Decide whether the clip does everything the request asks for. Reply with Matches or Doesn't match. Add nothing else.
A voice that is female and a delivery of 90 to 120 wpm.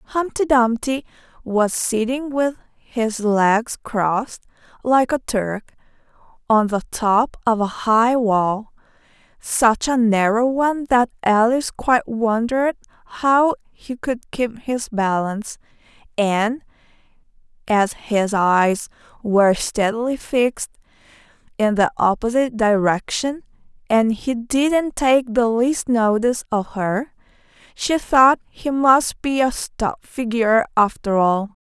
Matches